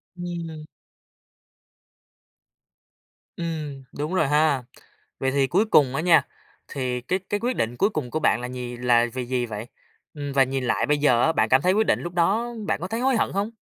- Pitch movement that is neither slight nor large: No, wide, 5.8 semitones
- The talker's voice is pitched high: No, medium, 150 Hz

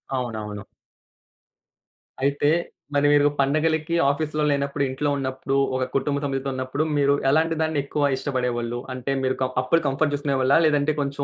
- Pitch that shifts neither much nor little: No, narrow, 2.1 semitones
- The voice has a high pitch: No, medium, 140 Hz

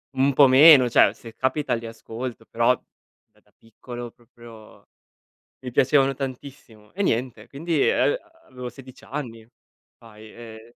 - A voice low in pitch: Yes, low, 125 Hz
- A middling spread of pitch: Yes, average, 3.0 semitones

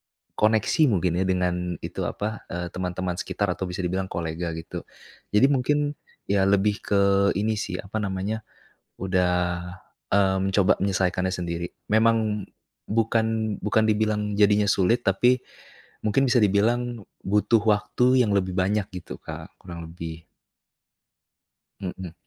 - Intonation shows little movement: No, average, 3.2 semitones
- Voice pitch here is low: Yes, low, 100 Hz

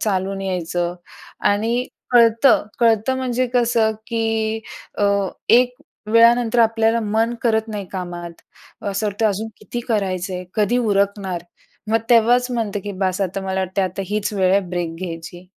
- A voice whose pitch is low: No, high, 210 Hz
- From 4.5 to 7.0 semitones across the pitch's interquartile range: No, average, 3.3 semitones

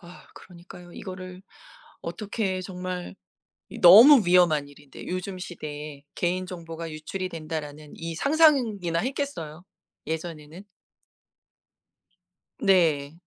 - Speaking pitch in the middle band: Yes, medium, 175 Hz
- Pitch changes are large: No, average, 2.9 semitones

